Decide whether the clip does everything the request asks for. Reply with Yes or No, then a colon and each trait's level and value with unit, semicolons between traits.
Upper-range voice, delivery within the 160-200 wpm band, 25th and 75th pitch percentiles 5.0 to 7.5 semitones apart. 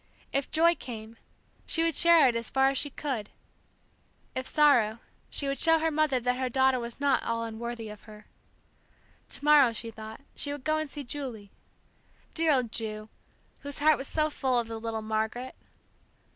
No: very high, 255 Hz; average, 185 wpm; average, 4.4 semitones